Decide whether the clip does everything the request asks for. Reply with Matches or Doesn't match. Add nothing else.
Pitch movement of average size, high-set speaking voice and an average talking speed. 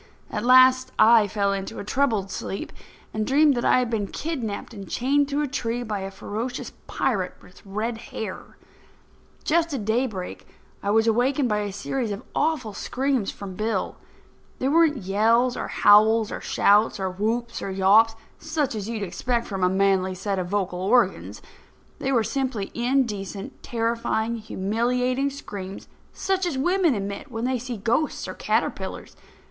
Matches